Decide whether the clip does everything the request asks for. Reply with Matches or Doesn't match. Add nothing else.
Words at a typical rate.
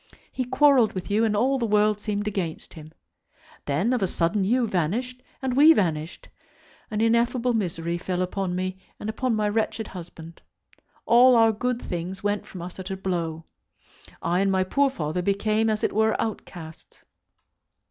Matches